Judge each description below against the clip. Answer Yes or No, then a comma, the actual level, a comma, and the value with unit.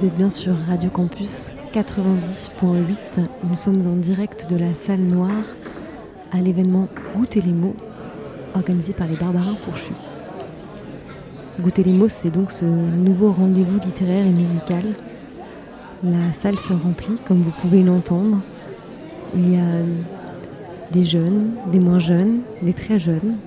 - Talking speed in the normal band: No, slow, 140 wpm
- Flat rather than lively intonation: Yes, narrow, 2.0 semitones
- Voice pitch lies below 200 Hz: Yes, medium, 185 Hz